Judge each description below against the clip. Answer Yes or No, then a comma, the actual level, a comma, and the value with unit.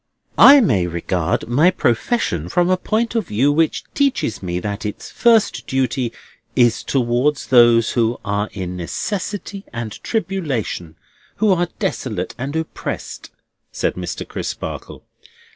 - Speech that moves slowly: Yes, slow, 130 wpm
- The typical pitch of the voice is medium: No, low, 125 Hz